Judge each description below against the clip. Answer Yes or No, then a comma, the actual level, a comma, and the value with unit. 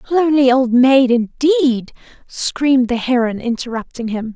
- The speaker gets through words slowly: Yes, slow, 125 wpm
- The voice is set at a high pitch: Yes, very high, 255 Hz